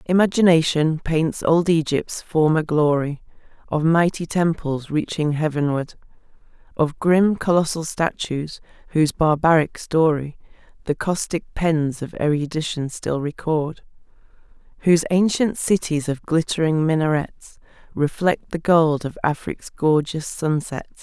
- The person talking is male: No, female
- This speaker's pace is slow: Yes, slow, 110 wpm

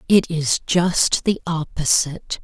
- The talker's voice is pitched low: No, medium, 165 Hz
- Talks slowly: Yes, slow, 125 wpm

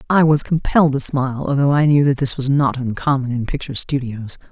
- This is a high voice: No, medium, 140 Hz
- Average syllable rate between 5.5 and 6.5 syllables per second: Yes, 6.0 syllables/s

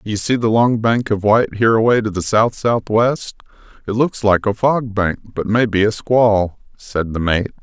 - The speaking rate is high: Yes, fast, 215 wpm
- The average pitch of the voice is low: Yes, low, 110 Hz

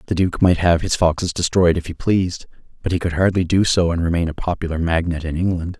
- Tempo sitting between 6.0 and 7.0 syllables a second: Yes, 6.3 syllables/s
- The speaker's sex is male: Yes, male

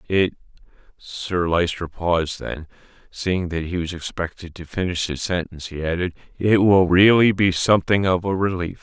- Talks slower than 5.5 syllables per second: Yes, 5.0 syllables/s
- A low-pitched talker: Yes, very low, 90 Hz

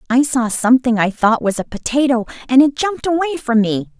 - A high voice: Yes, very high, 250 Hz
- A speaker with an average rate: No, fast, 210 wpm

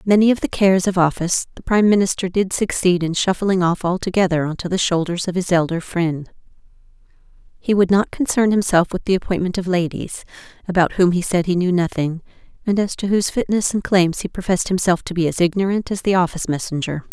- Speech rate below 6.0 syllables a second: No, 6.1 syllables/s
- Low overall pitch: No, medium, 180 Hz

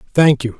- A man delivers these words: Yes, male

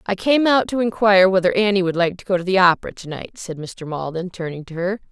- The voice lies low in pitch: No, high, 190 Hz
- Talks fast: Yes, fast, 245 wpm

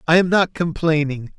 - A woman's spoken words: No, male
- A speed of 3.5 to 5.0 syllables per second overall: Yes, 4.9 syllables/s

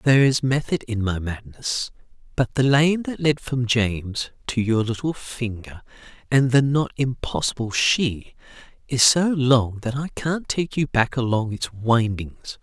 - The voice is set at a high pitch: No, low, 125 Hz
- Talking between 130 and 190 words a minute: Yes, average, 160 wpm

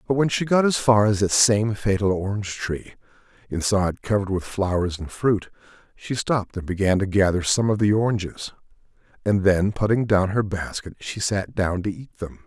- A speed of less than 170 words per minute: No, average, 195 wpm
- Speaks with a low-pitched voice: Yes, low, 100 Hz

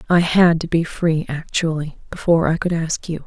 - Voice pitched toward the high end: No, medium, 165 Hz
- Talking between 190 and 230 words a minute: Yes, average, 200 wpm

